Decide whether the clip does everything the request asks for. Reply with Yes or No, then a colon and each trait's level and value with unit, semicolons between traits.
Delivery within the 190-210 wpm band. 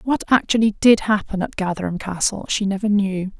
No: average, 175 wpm